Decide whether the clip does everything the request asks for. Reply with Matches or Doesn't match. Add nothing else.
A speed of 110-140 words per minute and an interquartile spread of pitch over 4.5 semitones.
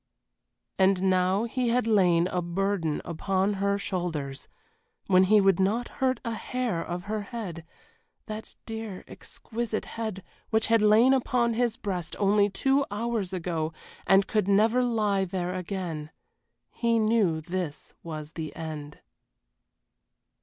Doesn't match